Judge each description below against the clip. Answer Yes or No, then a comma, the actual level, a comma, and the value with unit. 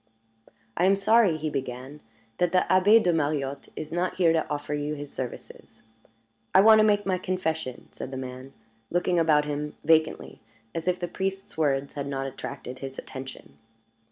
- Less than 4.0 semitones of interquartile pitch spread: No, average, 5.0 semitones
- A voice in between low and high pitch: Yes, medium, 155 Hz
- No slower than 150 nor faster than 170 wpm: No, average, 180 wpm